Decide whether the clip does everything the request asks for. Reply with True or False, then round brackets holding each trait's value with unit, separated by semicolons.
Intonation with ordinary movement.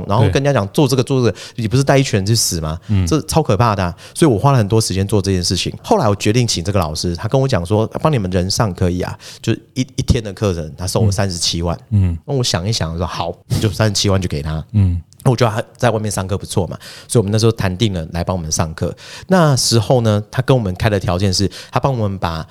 True (4.9 semitones)